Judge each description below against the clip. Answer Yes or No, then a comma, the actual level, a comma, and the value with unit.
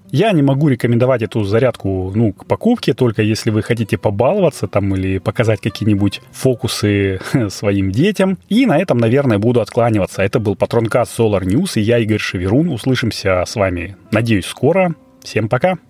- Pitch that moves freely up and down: No, average, 4.3 semitones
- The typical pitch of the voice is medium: No, low, 115 Hz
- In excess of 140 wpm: Yes, fast, 160 wpm